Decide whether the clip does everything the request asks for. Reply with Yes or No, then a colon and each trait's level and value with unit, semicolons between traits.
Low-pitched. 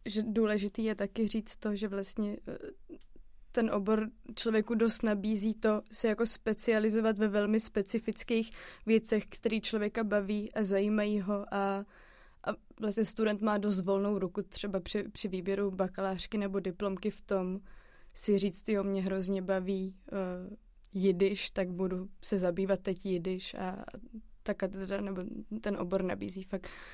No: high, 205 Hz